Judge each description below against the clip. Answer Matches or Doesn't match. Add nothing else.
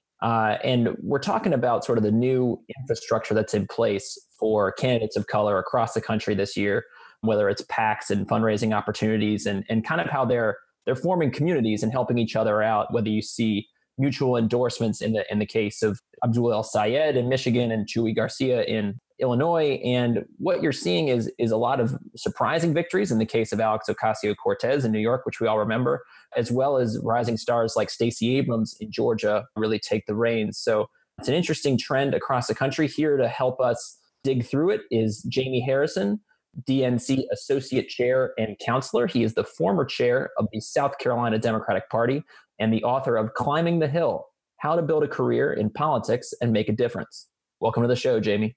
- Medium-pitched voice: Doesn't match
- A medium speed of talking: Matches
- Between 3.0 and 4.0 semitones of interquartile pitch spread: Matches